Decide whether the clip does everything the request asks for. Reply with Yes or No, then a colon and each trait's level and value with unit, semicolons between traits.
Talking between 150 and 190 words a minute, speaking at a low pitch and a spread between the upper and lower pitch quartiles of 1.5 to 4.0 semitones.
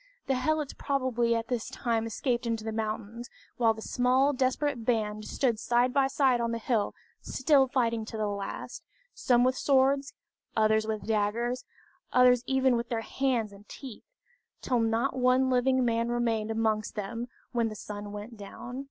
No: average, 170 wpm; high, 235 Hz; average, 2.7 semitones